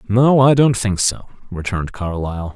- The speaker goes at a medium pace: Yes, average, 165 wpm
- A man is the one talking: Yes, male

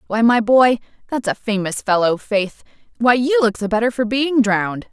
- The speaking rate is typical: Yes, average, 170 wpm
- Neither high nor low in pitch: No, high, 225 Hz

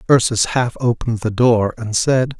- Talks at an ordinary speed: Yes, average, 175 wpm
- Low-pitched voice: Yes, low, 115 Hz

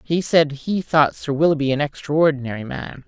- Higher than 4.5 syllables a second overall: Yes, 5.1 syllables/s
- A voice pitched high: No, medium, 150 Hz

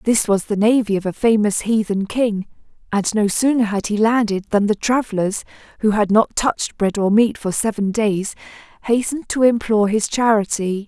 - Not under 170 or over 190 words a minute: Yes, average, 180 wpm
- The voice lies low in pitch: No, high, 215 Hz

